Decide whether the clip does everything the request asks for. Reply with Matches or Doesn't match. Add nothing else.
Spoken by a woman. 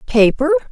Matches